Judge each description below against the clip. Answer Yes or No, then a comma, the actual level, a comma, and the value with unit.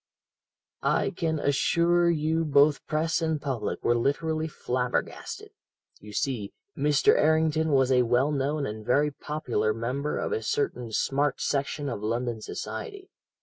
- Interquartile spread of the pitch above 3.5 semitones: Yes, average, 4.2 semitones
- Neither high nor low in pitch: Yes, medium, 145 Hz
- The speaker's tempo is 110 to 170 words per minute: Yes, average, 140 wpm